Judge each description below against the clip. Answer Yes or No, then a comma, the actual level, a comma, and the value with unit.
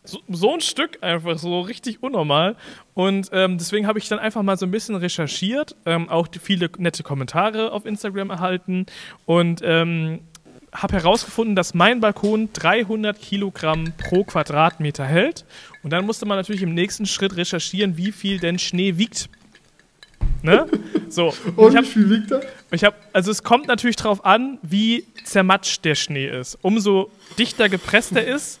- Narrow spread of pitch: No, average, 3.8 semitones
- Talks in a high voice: Yes, high, 195 Hz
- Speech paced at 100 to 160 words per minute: Yes, average, 155 wpm